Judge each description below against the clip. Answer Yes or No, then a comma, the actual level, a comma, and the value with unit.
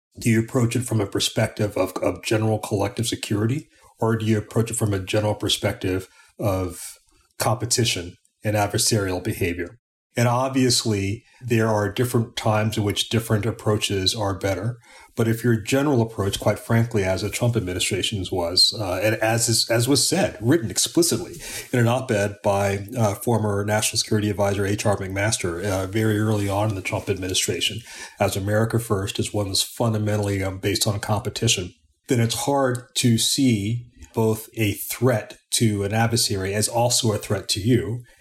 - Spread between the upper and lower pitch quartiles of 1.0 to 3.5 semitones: Yes, narrow, 2.4 semitones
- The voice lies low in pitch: Yes, low, 110 Hz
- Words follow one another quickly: No, average, 170 wpm